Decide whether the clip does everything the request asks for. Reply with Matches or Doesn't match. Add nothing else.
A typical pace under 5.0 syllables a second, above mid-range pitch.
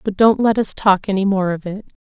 Doesn't match